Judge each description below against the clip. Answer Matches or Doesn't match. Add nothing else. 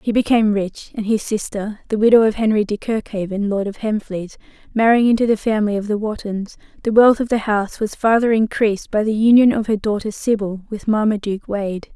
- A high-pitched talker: Matches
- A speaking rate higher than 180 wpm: Matches